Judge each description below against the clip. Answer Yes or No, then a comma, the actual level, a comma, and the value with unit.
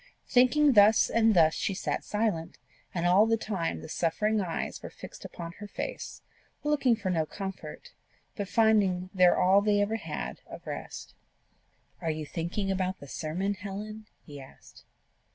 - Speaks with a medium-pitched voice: No, high, 195 Hz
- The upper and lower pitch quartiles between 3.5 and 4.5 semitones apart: Yes, average, 3.9 semitones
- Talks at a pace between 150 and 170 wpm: Yes, average, 160 wpm